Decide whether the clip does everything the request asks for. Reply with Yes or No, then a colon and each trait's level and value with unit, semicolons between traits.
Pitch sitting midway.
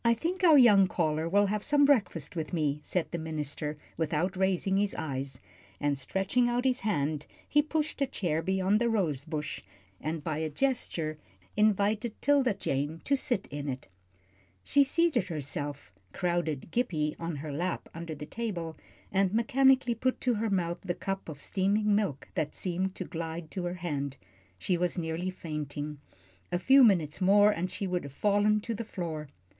Yes: medium, 180 Hz